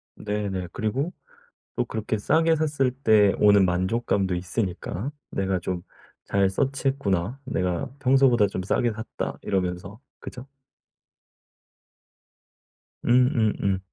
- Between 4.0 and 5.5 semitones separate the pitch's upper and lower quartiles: Yes, average, 5.2 semitones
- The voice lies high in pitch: No, low, 105 Hz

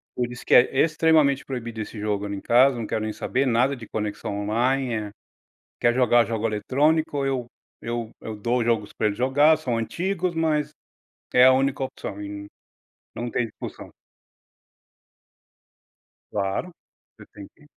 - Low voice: Yes, low, 120 Hz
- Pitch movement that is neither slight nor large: Yes, average, 4.1 semitones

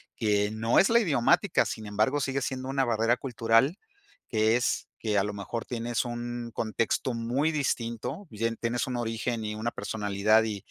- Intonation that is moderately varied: No, narrow, 2.3 semitones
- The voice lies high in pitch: No, low, 115 Hz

